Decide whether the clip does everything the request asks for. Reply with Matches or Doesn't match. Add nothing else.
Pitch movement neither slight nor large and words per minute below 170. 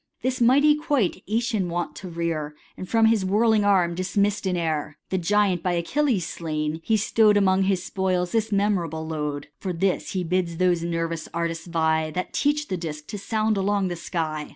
Doesn't match